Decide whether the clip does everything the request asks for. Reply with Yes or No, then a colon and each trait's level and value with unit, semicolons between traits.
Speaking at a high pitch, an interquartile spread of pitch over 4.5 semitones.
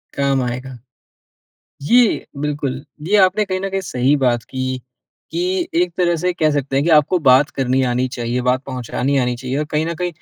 No: medium, 140 Hz; average, 5.1 semitones